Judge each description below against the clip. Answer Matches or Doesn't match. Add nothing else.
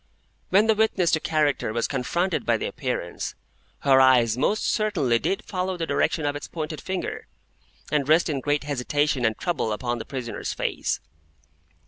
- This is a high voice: Doesn't match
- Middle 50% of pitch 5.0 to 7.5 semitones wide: Matches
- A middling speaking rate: Matches